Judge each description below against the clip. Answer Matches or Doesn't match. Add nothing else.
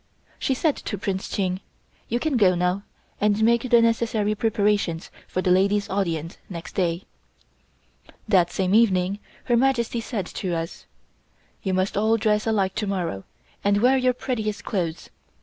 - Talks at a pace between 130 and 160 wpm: Matches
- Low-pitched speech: Doesn't match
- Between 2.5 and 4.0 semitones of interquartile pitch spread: Matches